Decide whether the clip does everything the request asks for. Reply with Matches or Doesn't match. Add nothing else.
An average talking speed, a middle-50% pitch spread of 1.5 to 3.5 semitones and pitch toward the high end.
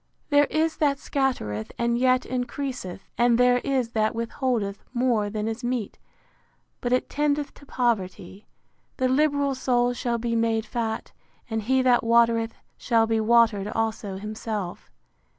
Matches